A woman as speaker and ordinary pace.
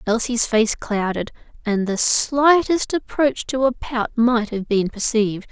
Yes: female; average, 150 wpm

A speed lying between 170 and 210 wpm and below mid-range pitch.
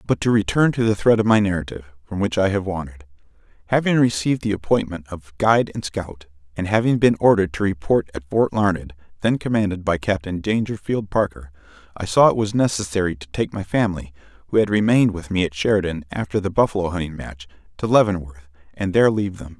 Yes: average, 190 wpm; very low, 95 Hz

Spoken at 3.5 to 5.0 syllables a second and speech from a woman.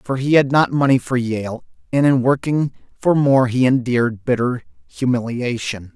No: 4.6 syllables/s; male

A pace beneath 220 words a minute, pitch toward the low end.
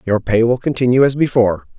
Yes: average, 200 wpm; low, 120 Hz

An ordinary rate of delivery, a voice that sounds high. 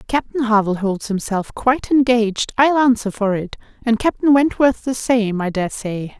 Yes: average, 175 wpm; high, 230 Hz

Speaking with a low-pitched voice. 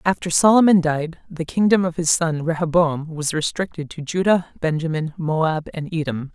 No: medium, 165 Hz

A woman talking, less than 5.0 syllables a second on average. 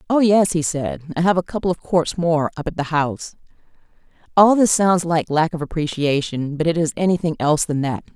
No: female; 5.6 syllables/s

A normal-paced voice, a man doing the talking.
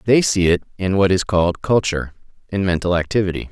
Yes: average, 170 wpm; male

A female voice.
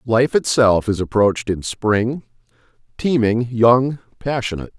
No: male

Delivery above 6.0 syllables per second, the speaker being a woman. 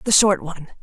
Yes: 6.8 syllables/s; female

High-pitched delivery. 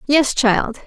Yes: very high, 255 Hz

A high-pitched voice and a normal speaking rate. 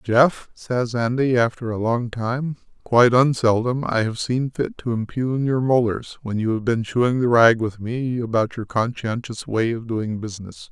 No: low, 120 Hz; average, 185 wpm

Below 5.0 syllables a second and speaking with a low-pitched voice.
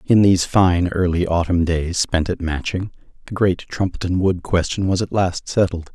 Yes: 4.8 syllables/s; very low, 90 Hz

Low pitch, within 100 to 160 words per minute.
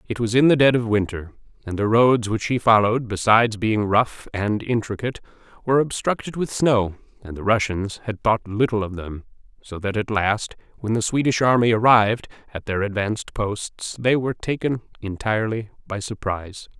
No: low, 110 Hz; average, 175 wpm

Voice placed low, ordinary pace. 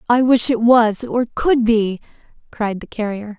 No: high, 230 Hz; average, 175 wpm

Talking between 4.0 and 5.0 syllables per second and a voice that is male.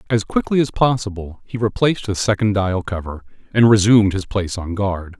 No: 5.6 syllables/s; male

